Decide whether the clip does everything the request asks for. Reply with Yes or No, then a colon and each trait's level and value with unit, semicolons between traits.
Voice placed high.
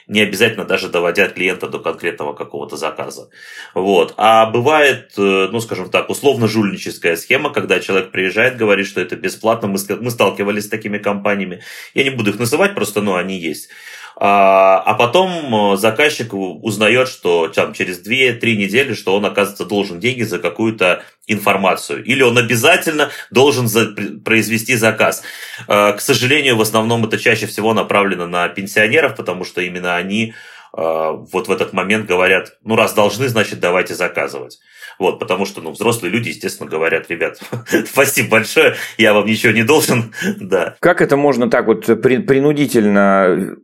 No: low, 110 Hz